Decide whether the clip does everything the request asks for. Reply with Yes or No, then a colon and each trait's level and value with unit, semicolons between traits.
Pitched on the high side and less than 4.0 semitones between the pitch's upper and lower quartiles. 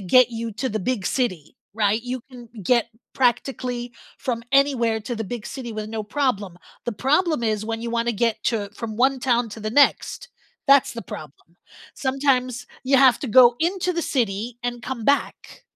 Yes: high, 240 Hz; average, 3.0 semitones